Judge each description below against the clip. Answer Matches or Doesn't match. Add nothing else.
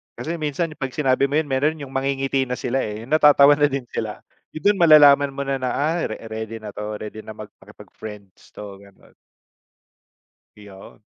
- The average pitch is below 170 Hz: Matches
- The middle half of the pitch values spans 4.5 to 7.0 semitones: Matches